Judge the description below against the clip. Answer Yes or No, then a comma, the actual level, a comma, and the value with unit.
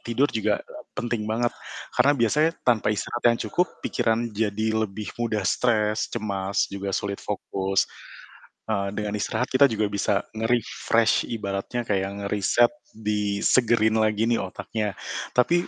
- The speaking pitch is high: No, low, 110 Hz